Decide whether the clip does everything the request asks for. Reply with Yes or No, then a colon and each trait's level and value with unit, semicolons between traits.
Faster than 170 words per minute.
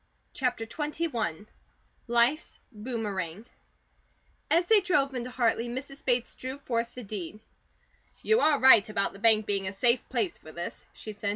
No: average, 155 wpm